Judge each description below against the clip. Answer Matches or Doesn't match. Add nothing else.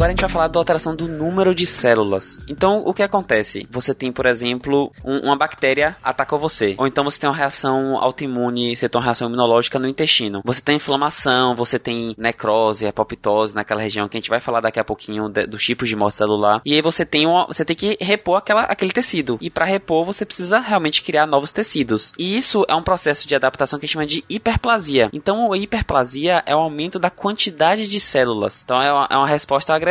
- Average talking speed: Doesn't match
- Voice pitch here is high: Doesn't match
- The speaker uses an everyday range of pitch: Doesn't match